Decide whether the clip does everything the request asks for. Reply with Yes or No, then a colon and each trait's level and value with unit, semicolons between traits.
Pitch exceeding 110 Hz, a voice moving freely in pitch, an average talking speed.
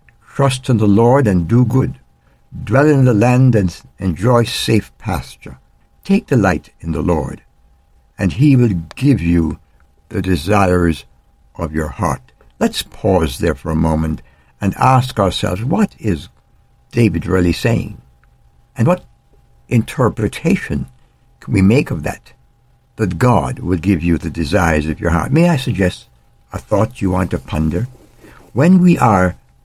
No: very low, 90 Hz; wide, 7.3 semitones; average, 150 wpm